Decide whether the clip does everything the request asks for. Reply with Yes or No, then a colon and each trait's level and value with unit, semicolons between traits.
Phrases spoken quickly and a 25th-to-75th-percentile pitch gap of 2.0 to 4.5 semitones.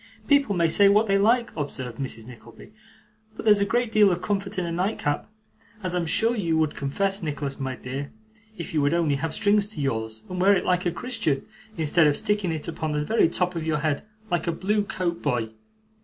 No: fast, 215 wpm; wide, 5.5 semitones